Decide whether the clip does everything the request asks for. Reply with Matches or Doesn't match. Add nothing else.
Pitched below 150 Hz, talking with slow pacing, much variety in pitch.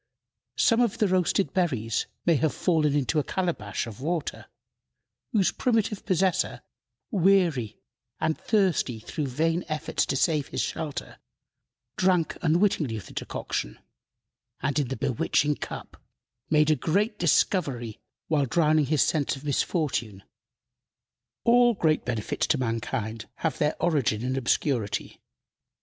Doesn't match